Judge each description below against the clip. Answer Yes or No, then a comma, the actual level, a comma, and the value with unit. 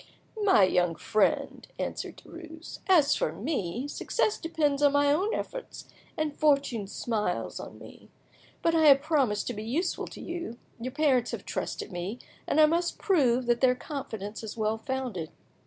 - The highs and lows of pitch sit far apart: Yes, wide, 6.0 semitones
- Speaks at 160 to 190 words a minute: Yes, average, 165 wpm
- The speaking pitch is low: No, very high, 275 Hz